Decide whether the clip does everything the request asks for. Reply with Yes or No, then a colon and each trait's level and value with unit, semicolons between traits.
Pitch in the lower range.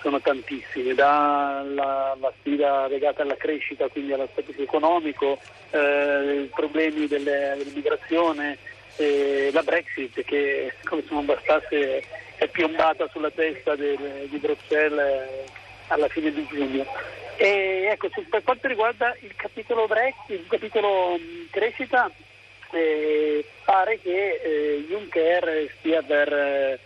No: medium, 150 Hz